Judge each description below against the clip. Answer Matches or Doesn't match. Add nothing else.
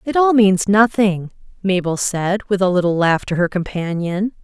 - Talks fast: Doesn't match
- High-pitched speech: Matches